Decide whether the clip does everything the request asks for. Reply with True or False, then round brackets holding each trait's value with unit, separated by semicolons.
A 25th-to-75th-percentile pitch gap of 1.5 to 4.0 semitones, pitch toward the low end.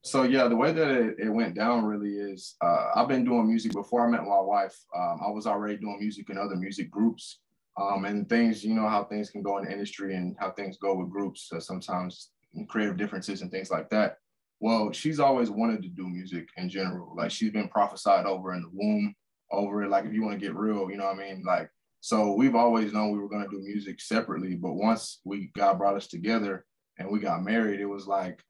True (2.5 semitones; 100 Hz)